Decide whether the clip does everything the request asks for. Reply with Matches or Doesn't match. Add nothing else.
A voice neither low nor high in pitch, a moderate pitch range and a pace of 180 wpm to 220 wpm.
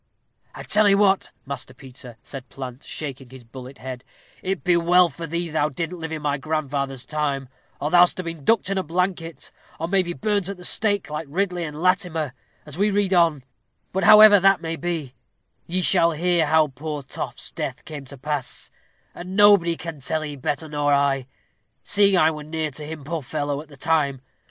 Matches